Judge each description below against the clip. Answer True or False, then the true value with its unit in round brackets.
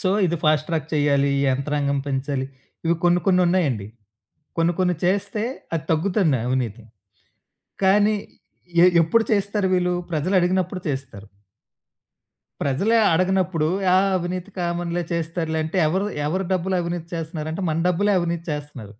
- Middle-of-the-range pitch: True (170 Hz)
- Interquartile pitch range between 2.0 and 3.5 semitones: False (3.9 semitones)